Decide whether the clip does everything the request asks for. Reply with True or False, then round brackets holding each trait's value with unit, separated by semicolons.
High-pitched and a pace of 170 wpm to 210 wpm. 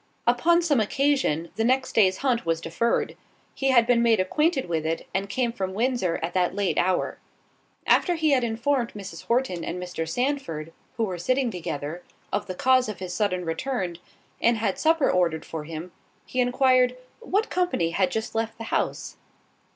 True (225 Hz; 180 wpm)